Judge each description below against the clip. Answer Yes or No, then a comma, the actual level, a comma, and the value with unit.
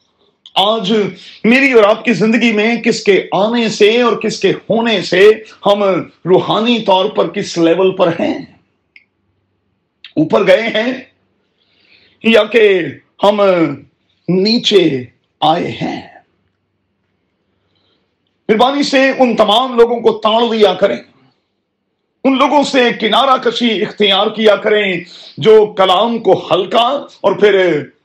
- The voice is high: Yes, high, 210 Hz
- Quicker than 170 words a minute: No, average, 120 wpm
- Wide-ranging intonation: No, average, 4.3 semitones